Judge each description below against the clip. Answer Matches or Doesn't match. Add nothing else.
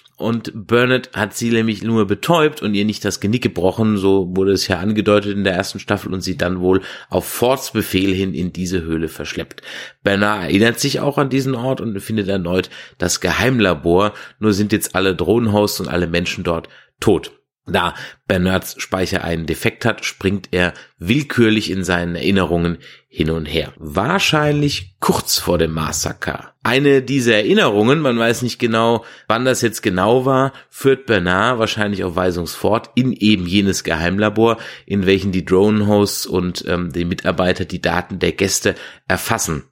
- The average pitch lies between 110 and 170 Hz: Doesn't match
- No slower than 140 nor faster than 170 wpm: Matches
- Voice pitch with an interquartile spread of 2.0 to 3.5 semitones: Doesn't match